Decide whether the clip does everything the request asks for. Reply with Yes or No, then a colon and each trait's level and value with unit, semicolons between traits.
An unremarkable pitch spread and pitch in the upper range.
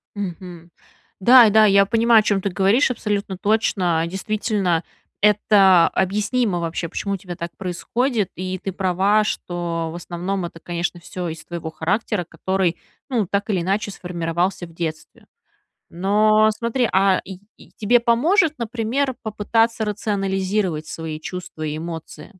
Yes: average, 3.7 semitones; high, 195 Hz